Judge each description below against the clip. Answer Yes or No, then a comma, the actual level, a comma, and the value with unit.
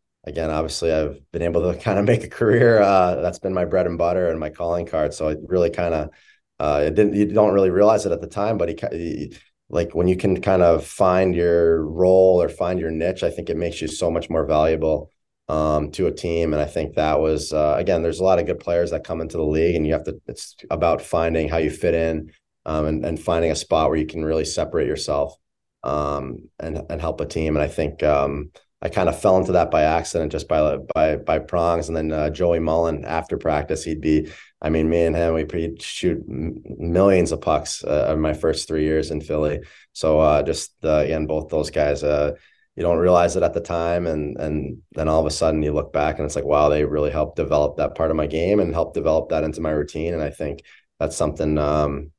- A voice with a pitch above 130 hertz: No, very low, 80 Hz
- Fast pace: Yes, fast, 245 wpm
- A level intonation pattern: Yes, narrow, 1.8 semitones